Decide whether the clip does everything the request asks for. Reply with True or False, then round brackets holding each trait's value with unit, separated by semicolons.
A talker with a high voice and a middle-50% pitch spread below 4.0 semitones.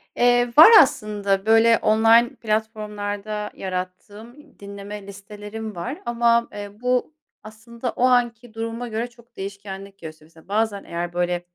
True (215 Hz; 2.9 semitones)